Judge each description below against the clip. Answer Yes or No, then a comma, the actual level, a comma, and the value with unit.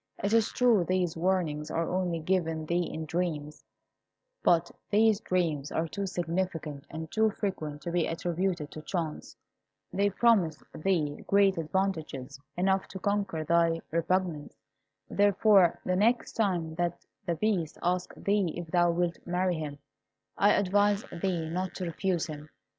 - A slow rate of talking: No, average, 145 wpm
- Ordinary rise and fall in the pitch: Yes, average, 3.1 semitones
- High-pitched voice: No, medium, 175 Hz